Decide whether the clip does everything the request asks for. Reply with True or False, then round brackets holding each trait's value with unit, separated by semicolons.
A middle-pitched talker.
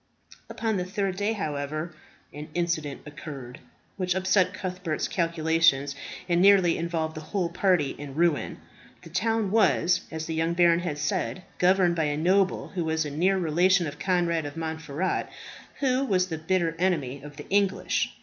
True (170 Hz)